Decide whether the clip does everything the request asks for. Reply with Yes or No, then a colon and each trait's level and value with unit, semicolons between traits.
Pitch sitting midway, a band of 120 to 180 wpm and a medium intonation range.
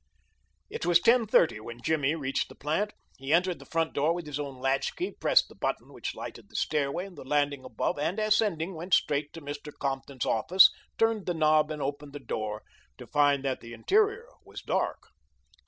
No: medium, 150 Hz; average, 195 wpm; average, 4.3 semitones